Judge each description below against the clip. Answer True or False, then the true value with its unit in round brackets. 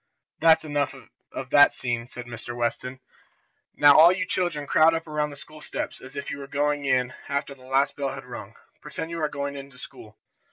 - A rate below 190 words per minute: False (205 wpm)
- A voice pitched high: False (140 Hz)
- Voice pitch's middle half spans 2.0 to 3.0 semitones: True (2.7 semitones)